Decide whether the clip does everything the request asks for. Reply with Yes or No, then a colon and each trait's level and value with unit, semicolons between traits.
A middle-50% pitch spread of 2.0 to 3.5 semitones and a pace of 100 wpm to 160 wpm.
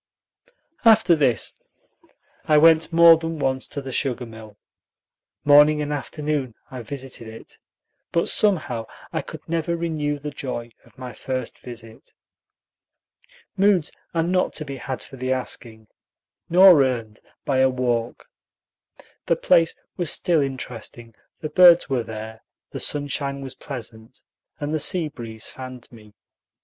No: average, 4.7 semitones; average, 140 wpm